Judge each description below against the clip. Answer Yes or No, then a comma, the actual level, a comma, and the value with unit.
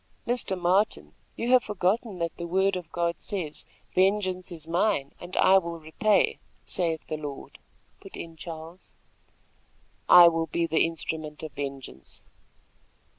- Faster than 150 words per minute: No, average, 140 wpm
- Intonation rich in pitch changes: No, average, 3.0 semitones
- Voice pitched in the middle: Yes, medium, 170 Hz